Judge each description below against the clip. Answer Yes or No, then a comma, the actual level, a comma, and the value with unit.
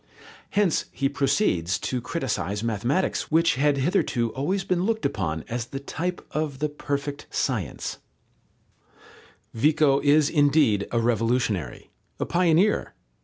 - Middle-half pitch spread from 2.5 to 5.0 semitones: No, wide, 5.5 semitones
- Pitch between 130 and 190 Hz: Yes, medium, 140 Hz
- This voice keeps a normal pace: No, slow, 120 wpm